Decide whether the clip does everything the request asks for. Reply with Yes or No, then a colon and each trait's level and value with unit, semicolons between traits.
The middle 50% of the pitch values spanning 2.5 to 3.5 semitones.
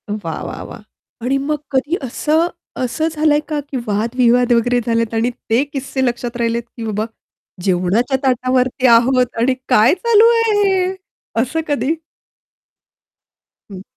No: average, 3.9 semitones